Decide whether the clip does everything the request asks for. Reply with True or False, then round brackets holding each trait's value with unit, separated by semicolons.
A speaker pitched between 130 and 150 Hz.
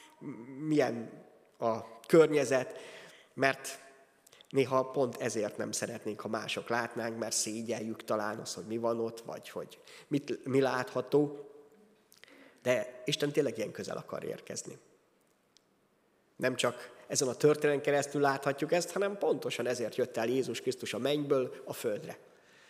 True (135 Hz)